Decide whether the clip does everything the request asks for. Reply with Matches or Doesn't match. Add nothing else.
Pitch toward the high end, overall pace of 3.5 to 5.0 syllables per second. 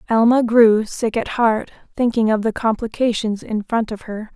Matches